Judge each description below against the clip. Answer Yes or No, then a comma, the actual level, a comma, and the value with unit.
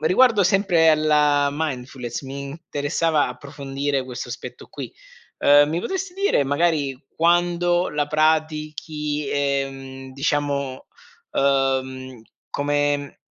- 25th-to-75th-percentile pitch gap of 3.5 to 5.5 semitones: No, narrow, 2.6 semitones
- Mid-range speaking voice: Yes, medium, 145 Hz